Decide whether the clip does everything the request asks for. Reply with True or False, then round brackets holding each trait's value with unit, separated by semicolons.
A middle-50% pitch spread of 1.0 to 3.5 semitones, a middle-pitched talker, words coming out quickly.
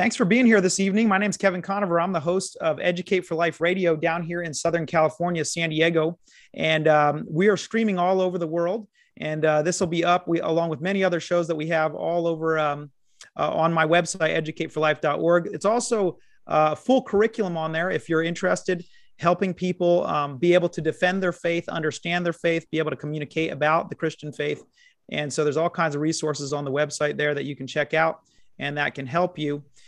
True (2.6 semitones; 170 Hz; 220 wpm)